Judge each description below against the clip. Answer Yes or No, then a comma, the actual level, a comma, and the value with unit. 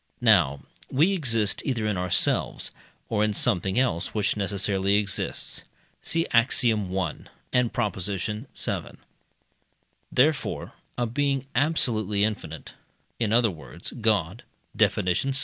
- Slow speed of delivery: Yes, slow, 115 wpm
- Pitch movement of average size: Yes, average, 4.5 semitones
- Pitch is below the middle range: Yes, low, 105 Hz